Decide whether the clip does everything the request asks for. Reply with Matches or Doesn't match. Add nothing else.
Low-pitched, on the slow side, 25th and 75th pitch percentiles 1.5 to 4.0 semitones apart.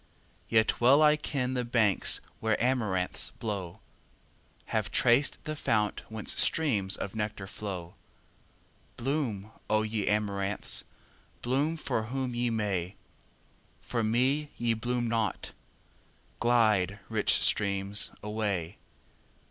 Matches